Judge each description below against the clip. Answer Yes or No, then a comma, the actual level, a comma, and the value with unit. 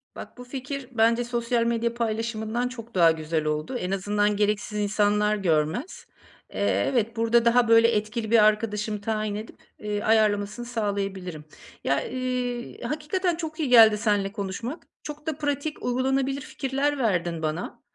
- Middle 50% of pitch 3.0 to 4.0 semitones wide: Yes, average, 3.3 semitones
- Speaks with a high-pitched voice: Yes, high, 225 Hz